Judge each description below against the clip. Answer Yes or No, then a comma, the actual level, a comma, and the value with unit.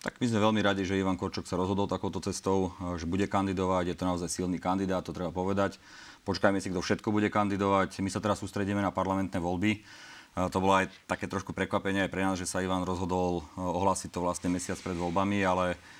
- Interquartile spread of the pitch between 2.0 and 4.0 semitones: No, narrow, 1.4 semitones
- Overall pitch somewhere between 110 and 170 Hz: No, very low, 95 Hz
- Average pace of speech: No, fast, 210 wpm